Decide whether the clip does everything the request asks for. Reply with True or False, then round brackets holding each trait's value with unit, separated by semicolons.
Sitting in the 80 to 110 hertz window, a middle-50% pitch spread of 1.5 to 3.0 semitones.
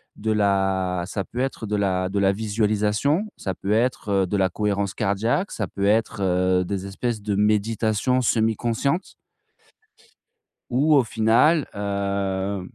True (105 Hz; 2.5 semitones)